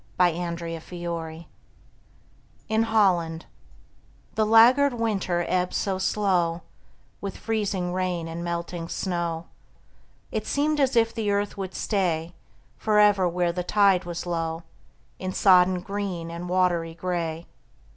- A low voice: No, medium, 180 Hz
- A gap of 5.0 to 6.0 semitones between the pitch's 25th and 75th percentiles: No, average, 3.2 semitones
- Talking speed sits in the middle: No, slow, 125 wpm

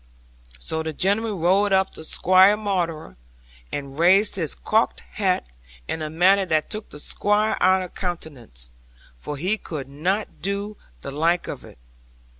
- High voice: No, medium, 180 Hz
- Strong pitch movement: No, average, 4.3 semitones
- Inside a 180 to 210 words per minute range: No, average, 155 wpm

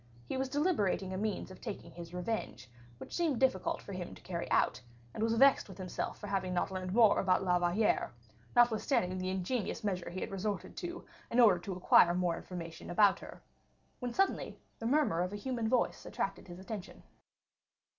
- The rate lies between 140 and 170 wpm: No, average, 190 wpm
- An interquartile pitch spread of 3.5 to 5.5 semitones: Yes, average, 4.1 semitones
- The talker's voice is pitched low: No, high, 195 Hz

